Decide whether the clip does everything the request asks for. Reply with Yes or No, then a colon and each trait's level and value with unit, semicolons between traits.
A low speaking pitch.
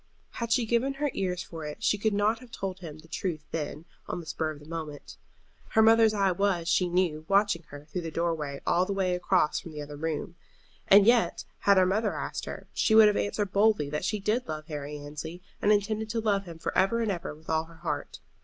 No: medium, 185 Hz